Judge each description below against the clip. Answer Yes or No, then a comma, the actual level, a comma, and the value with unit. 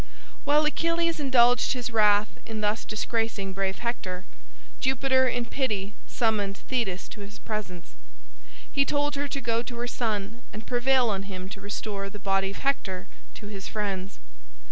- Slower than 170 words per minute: Yes, average, 160 wpm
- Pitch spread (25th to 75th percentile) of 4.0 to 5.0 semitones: Yes, average, 4.4 semitones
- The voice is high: Yes, high, 220 Hz